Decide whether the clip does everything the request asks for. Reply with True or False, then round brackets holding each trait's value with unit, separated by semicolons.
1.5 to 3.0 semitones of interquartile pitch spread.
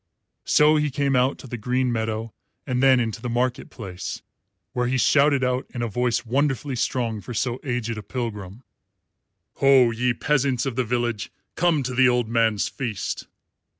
True (2.4 semitones)